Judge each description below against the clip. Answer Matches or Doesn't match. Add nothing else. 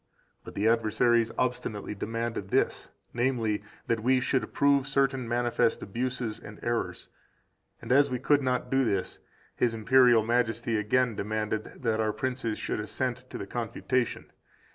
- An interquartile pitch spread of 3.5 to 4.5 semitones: Doesn't match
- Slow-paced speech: Doesn't match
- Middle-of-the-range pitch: Doesn't match